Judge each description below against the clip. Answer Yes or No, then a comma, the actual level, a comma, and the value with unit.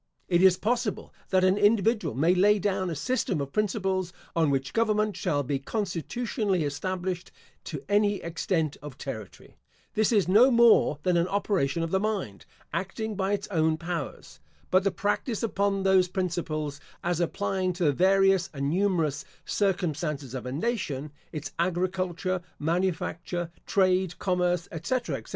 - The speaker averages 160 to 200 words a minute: No, average, 150 wpm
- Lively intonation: No, average, 3.8 semitones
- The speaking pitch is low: No, medium, 185 Hz